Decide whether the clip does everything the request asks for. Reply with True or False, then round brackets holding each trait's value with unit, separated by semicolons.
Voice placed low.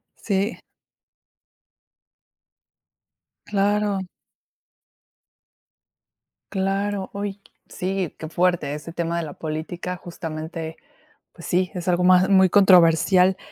False (180 Hz)